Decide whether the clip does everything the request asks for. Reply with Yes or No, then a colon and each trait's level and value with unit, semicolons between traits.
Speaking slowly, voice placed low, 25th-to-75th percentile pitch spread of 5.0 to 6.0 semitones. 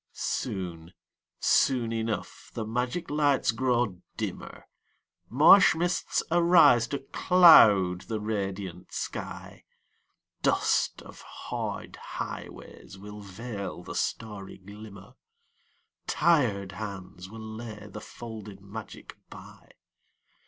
No: slow, 95 wpm; low, 110 Hz; average, 4.0 semitones